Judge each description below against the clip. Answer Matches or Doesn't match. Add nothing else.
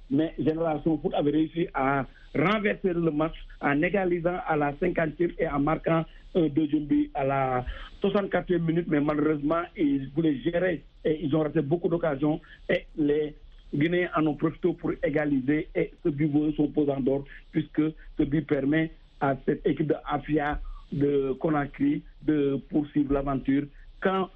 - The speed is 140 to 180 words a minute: Matches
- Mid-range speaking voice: Matches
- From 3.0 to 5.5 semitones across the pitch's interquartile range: Doesn't match